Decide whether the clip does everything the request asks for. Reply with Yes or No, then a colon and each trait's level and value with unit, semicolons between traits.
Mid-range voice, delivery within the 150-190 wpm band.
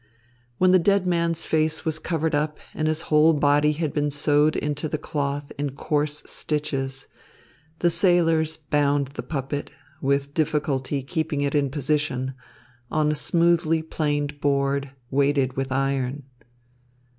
No: medium, 150 Hz; average, 140 wpm